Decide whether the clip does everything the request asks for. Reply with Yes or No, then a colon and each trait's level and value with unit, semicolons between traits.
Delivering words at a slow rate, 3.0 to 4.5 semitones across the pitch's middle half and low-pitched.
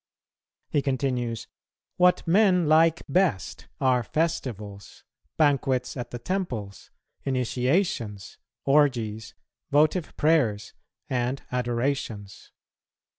No: slow, 80 wpm; average, 5.1 semitones; low, 130 Hz